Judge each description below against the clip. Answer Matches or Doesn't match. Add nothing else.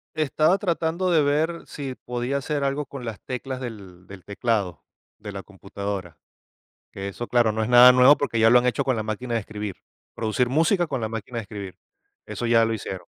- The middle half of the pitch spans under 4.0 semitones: Doesn't match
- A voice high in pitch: Doesn't match